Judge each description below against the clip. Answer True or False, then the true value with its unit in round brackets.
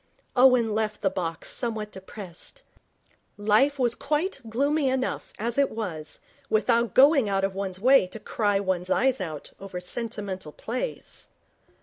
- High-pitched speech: True (220 Hz)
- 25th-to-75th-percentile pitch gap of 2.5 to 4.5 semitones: False (5.2 semitones)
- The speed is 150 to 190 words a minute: False (140 wpm)